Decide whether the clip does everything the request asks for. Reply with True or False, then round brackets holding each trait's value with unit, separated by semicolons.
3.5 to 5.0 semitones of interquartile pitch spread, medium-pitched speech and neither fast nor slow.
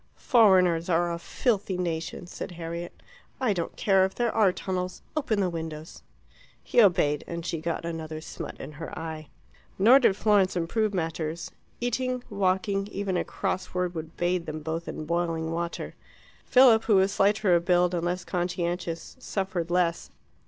False (2.9 semitones; 180 Hz; 165 wpm)